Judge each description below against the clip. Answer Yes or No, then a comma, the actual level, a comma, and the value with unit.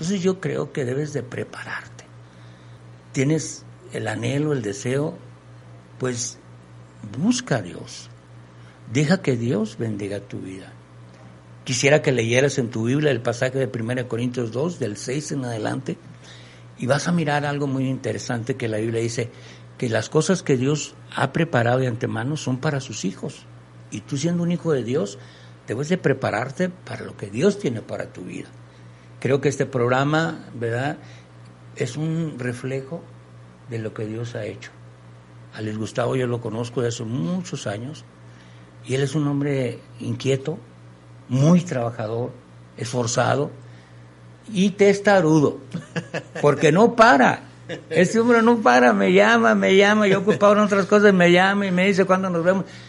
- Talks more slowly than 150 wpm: No, average, 155 wpm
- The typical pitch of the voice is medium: No, low, 125 Hz